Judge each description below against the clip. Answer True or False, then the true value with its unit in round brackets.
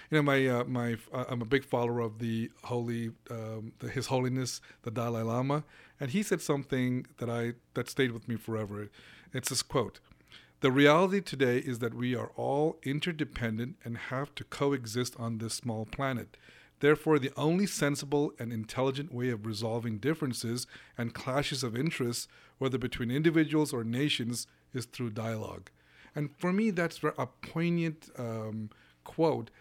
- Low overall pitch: True (125 Hz)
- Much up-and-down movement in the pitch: False (3.7 semitones)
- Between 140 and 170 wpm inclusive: True (165 wpm)